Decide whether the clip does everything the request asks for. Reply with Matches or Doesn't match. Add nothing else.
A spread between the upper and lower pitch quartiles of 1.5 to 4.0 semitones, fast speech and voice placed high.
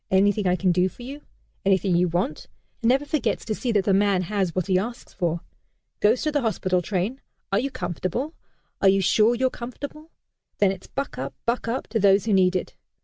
Doesn't match